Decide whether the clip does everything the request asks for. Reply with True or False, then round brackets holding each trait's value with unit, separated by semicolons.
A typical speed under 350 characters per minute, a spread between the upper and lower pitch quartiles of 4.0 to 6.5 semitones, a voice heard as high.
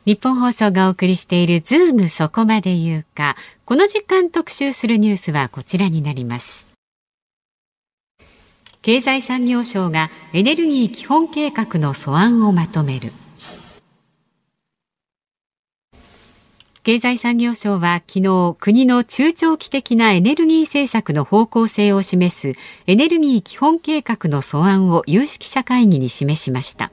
False (265 characters per minute; 7.0 semitones; 210 Hz)